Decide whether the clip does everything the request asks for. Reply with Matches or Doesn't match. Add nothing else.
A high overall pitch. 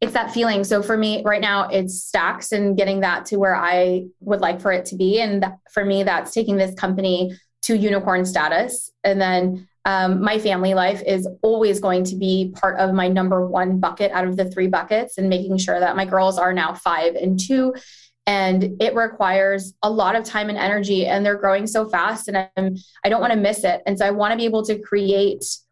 Matches